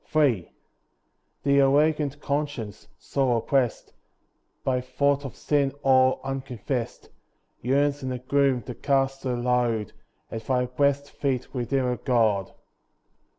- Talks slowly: Yes, slow, 115 wpm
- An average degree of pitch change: No, narrow, 2.3 semitones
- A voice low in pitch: Yes, low, 130 Hz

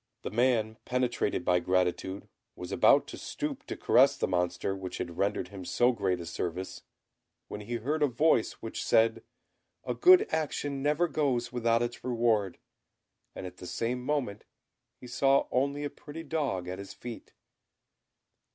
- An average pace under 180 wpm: Yes, average, 160 wpm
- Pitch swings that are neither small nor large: No, wide, 6.4 semitones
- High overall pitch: No, low, 115 Hz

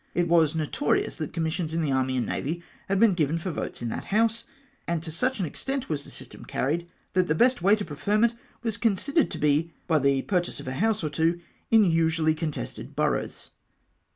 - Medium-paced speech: No, fast, 210 wpm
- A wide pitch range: No, average, 4.9 semitones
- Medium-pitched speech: Yes, medium, 165 Hz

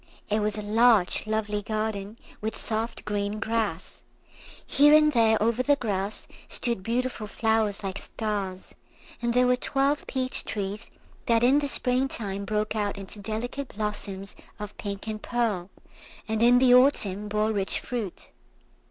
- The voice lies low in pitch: No, high, 220 Hz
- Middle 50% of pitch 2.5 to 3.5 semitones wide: Yes, average, 2.9 semitones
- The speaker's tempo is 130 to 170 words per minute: Yes, average, 150 wpm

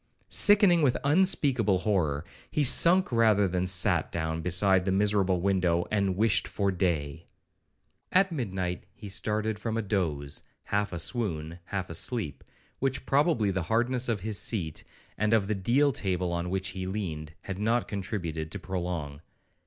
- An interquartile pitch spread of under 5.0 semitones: Yes, average, 4.3 semitones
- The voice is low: Yes, very low, 95 Hz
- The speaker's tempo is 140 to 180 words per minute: Yes, average, 160 wpm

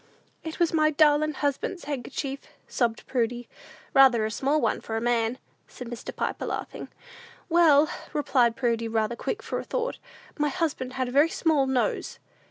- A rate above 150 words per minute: Yes, average, 165 wpm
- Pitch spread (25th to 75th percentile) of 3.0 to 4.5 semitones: Yes, average, 4.2 semitones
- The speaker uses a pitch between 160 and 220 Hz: No, very high, 270 Hz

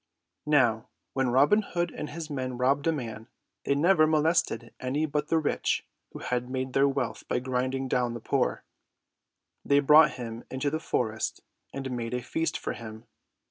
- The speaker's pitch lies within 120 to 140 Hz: Yes, low, 135 Hz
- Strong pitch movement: No, average, 3.5 semitones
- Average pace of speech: Yes, average, 180 wpm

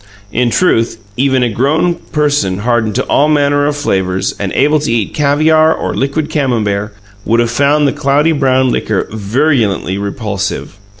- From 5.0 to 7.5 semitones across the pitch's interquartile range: Yes, wide, 5.4 semitones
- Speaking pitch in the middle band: No, low, 130 Hz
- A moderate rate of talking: Yes, average, 160 wpm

